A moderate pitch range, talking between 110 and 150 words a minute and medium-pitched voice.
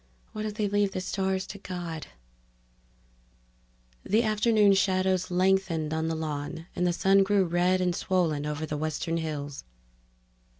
Yes: average, 3.3 semitones; average, 145 wpm; medium, 180 Hz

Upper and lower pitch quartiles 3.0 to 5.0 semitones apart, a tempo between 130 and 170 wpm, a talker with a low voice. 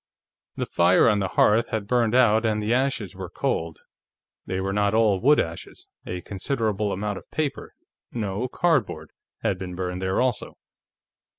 Yes: average, 3.9 semitones; average, 165 wpm; low, 105 Hz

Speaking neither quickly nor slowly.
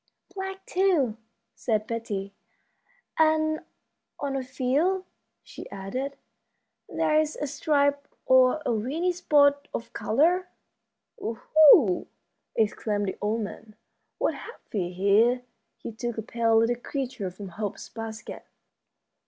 No: slow, 115 wpm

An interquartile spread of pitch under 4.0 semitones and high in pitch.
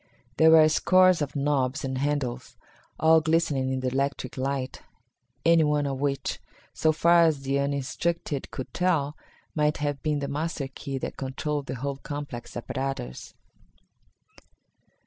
No: narrow, 2.6 semitones; medium, 140 Hz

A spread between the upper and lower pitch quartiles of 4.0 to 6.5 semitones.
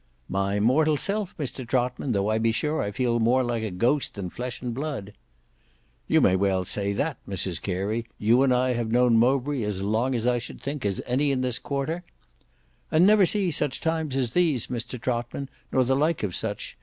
Yes: average, 4.3 semitones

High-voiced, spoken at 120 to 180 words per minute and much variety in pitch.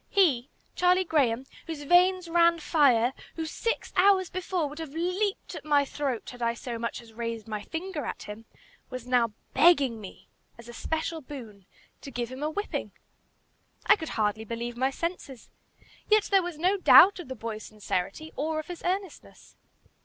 Yes: very high, 290 Hz; average, 175 wpm; wide, 7.0 semitones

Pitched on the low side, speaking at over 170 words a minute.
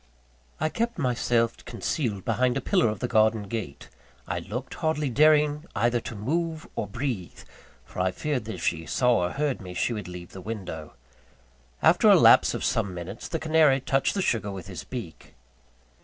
Yes: low, 115 Hz; average, 185 wpm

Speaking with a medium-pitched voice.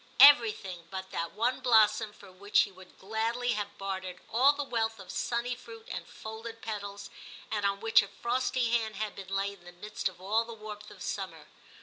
No: high, 215 Hz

